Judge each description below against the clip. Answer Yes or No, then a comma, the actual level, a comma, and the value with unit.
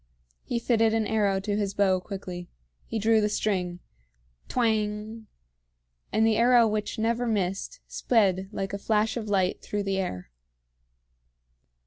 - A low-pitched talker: No, high, 210 Hz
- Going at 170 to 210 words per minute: No, average, 140 wpm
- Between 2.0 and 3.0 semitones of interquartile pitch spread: Yes, narrow, 2.4 semitones